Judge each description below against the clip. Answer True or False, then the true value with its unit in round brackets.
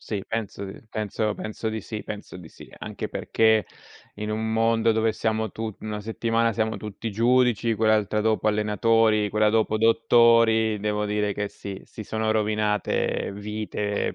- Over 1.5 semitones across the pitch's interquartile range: False (1.1 semitones)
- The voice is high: False (110 Hz)